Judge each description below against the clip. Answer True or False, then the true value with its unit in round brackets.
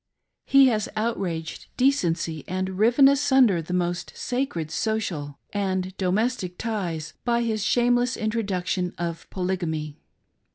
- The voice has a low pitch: False (190 Hz)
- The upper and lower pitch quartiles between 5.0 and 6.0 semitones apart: True (5.3 semitones)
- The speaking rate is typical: False (115 wpm)